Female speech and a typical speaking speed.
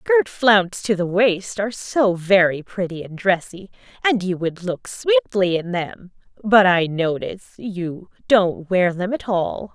Yes: female; average, 165 wpm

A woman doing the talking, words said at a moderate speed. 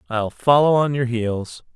No: male; average, 170 wpm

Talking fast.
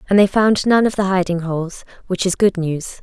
Yes: fast, 240 wpm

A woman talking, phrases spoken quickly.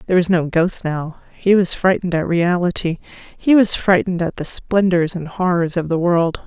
No: female; average, 195 wpm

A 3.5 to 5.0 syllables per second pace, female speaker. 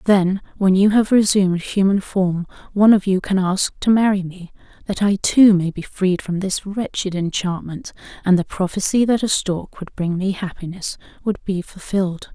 Yes: 4.8 syllables/s; female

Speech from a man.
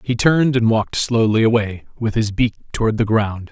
Yes: male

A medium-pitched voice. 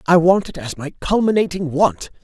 Yes: medium, 170 Hz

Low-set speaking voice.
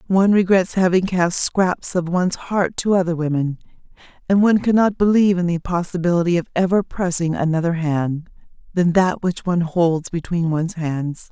No: medium, 175 Hz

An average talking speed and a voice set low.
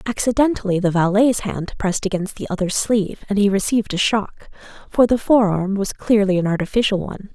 No: average, 180 wpm; high, 205 Hz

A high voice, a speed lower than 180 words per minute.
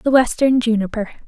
Yes: high, 235 Hz; average, 140 wpm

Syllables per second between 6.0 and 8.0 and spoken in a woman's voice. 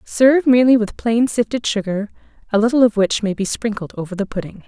Yes: 6.1 syllables/s; female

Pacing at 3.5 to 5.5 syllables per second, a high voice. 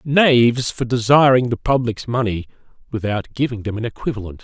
No: 5.4 syllables/s; low, 120 Hz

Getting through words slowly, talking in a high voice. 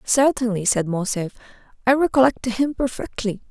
Yes: slow, 120 wpm; high, 235 Hz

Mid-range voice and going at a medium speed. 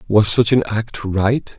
No: low, 105 Hz; average, 190 wpm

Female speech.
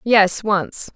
Yes: female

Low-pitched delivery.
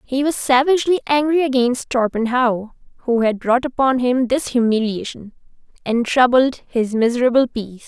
No: very high, 250 Hz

